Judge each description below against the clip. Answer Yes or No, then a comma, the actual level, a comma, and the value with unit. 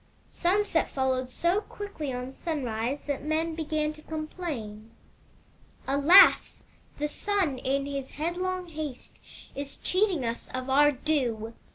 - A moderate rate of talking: No, slow, 130 wpm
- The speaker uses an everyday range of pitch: Yes, average, 4.2 semitones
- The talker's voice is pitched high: Yes, very high, 295 Hz